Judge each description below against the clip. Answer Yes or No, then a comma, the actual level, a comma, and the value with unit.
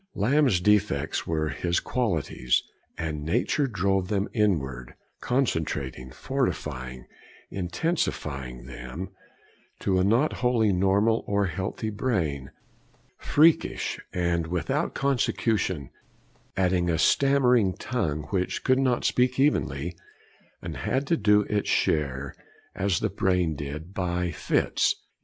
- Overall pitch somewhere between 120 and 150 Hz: No, very low, 95 Hz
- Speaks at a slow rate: Yes, slow, 115 wpm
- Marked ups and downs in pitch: Yes, wide, 6.7 semitones